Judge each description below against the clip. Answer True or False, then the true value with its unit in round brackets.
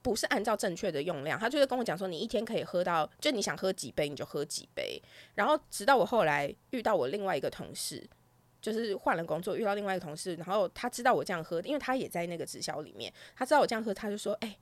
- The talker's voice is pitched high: True (205 Hz)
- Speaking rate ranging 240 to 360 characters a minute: False (395 characters per minute)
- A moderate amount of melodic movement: False (6.3 semitones)